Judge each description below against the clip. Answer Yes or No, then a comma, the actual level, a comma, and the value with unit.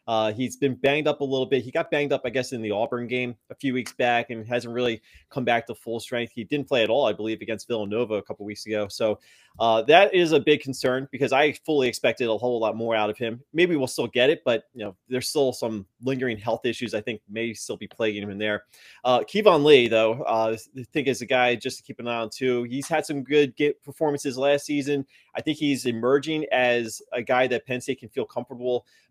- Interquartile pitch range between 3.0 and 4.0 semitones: Yes, average, 3.4 semitones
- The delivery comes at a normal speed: No, fast, 255 wpm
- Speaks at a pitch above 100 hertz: Yes, low, 125 Hz